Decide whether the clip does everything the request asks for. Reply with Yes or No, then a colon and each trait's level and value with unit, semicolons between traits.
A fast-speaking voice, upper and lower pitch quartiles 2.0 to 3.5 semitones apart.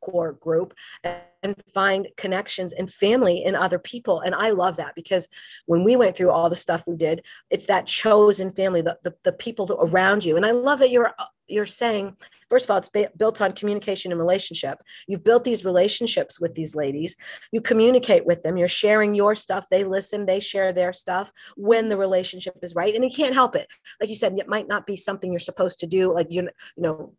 Yes: fast, 215 wpm; average, 3.0 semitones